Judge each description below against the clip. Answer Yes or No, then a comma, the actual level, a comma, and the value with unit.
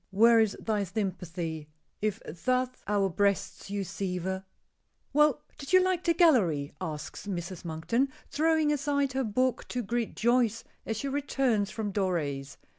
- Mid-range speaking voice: No, high, 215 Hz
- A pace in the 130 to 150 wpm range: Yes, average, 145 wpm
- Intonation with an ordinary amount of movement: No, wide, 6.0 semitones